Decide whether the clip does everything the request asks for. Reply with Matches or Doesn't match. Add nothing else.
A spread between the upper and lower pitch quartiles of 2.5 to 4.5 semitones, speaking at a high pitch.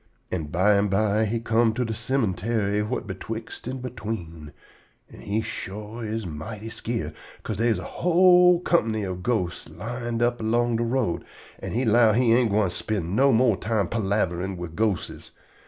Doesn't match